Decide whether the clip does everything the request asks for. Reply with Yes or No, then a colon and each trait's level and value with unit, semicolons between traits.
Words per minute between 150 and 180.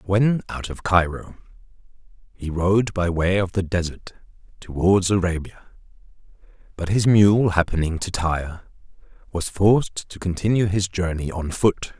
No: slow, 135 wpm